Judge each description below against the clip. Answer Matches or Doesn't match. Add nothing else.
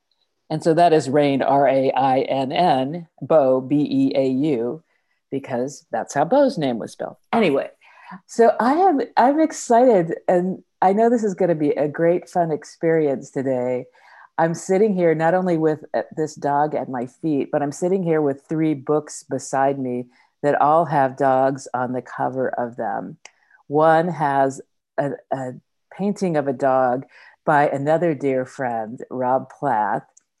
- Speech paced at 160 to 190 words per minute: Matches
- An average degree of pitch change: Matches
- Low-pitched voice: Doesn't match